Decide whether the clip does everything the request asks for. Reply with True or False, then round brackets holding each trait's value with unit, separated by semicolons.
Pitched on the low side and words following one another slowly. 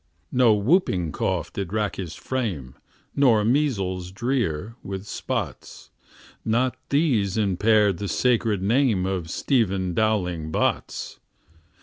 True (105 Hz; 110 wpm)